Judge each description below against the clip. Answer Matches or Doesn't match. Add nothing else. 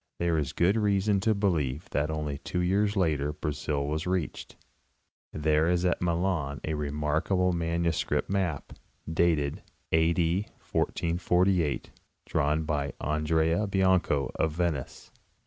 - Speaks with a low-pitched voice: Matches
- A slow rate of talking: Matches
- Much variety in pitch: Doesn't match